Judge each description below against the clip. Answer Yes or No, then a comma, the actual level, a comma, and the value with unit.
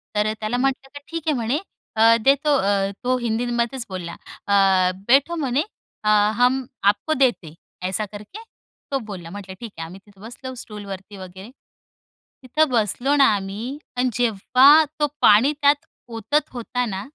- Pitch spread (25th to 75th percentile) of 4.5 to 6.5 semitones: Yes, average, 4.9 semitones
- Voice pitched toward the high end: Yes, high, 235 Hz